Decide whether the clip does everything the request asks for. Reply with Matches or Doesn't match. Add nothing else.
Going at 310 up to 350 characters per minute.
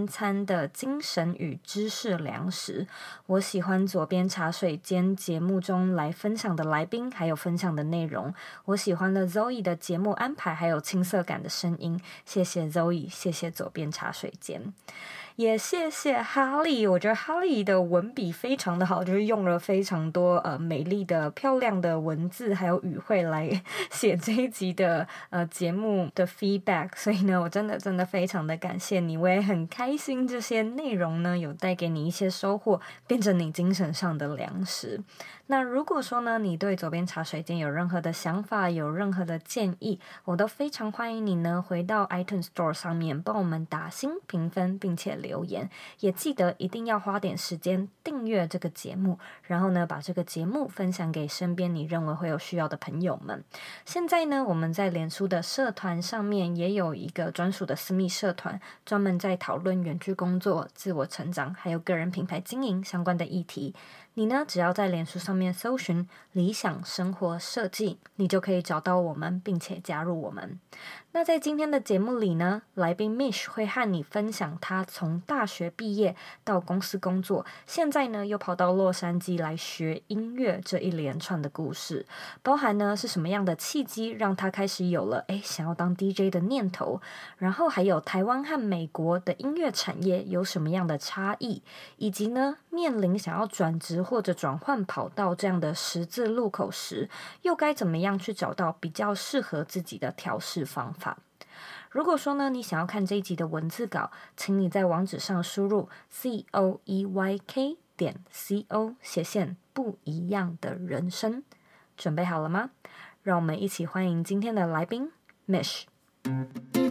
Doesn't match